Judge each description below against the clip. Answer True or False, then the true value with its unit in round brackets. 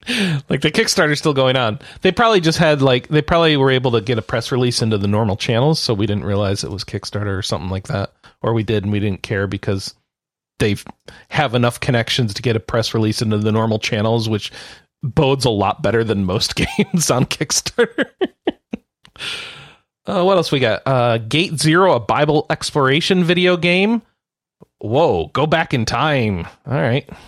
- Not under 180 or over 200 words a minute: True (190 wpm)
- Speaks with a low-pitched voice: True (125 Hz)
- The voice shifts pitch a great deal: True (6.3 semitones)